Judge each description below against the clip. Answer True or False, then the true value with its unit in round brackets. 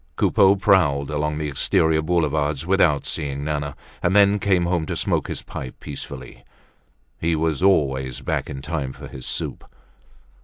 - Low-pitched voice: True (75 Hz)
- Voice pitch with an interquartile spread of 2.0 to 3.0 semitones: False (3.8 semitones)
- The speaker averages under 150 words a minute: False (155 wpm)